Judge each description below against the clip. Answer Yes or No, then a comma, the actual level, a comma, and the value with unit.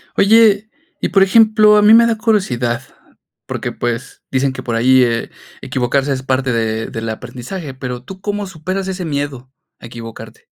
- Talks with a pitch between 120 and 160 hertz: Yes, low, 135 Hz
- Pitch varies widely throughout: Yes, wide, 8.3 semitones